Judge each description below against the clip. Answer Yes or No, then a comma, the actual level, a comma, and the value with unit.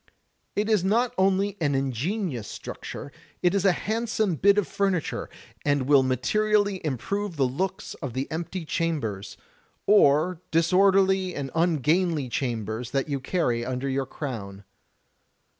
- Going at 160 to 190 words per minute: No, slow, 135 wpm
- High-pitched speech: No, medium, 165 Hz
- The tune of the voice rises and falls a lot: Yes, wide, 6.4 semitones